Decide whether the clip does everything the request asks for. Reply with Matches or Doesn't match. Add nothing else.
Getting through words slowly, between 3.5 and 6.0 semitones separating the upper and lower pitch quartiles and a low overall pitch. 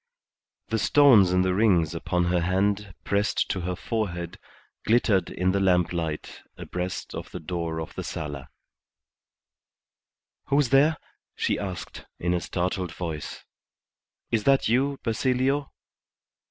Matches